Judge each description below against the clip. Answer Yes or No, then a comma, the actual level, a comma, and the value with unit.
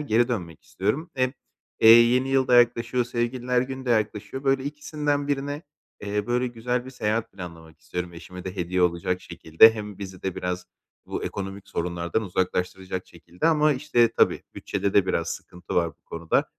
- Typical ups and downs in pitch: No, wide, 5.8 semitones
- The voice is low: Yes, low, 110 Hz